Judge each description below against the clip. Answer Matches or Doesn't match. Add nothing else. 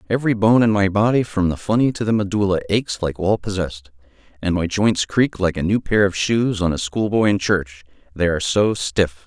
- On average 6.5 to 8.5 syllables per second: Doesn't match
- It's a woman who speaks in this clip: Doesn't match